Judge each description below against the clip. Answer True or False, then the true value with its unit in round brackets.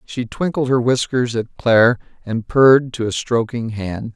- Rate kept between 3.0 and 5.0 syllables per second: True (4.5 syllables/s)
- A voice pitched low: True (120 Hz)